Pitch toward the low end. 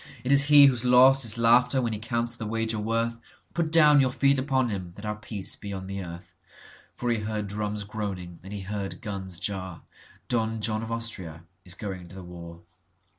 Yes: low, 110 Hz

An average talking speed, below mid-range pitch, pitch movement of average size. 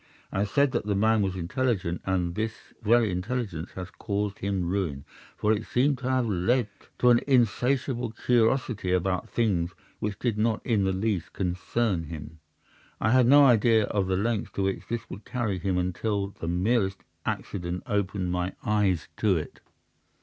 Yes: average, 170 wpm; low, 100 Hz; average, 4.2 semitones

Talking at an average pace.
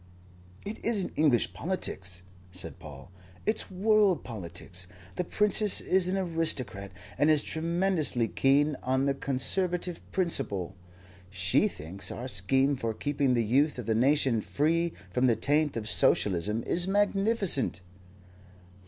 No: slow, 130 wpm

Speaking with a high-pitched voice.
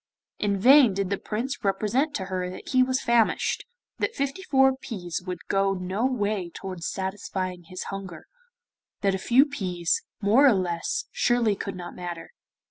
Yes: high, 200 Hz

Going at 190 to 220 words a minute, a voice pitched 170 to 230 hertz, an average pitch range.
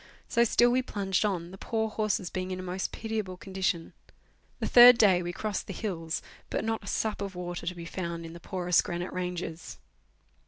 Yes: average, 200 wpm; medium, 185 Hz; average, 3.4 semitones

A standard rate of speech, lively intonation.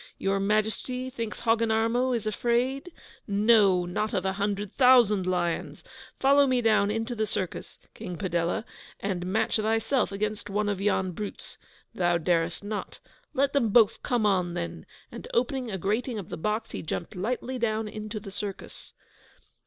No: average, 160 wpm; average, 3.4 semitones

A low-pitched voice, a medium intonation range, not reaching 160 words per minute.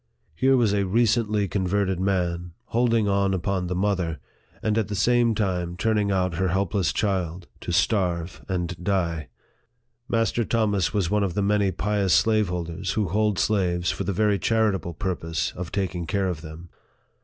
No: very low, 95 Hz; average, 3.1 semitones; average, 165 wpm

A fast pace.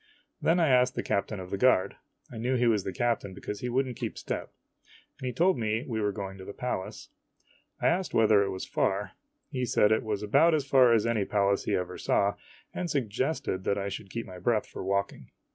Yes: fast, 230 wpm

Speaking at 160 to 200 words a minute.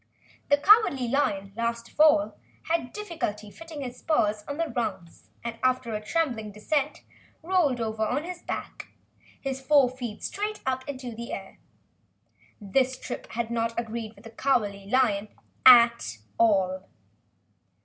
No: average, 145 wpm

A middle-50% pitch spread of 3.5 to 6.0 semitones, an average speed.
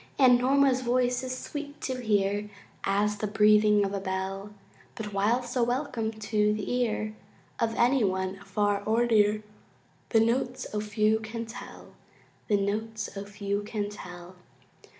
No: average, 2.9 semitones; average, 150 wpm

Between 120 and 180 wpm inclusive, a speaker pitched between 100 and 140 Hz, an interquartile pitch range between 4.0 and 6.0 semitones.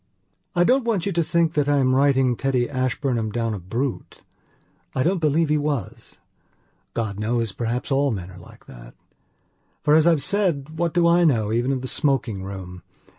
No: average, 190 wpm; low, 135 Hz; wide, 5.5 semitones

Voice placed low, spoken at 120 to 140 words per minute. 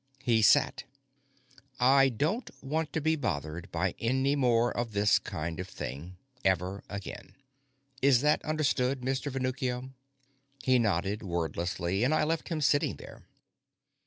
Yes: low, 125 Hz; slow, 135 wpm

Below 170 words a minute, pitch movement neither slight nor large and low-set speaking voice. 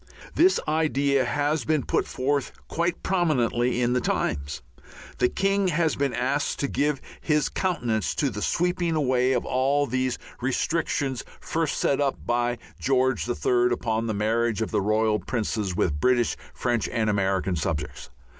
Yes: average, 155 wpm; average, 4.5 semitones; low, 125 Hz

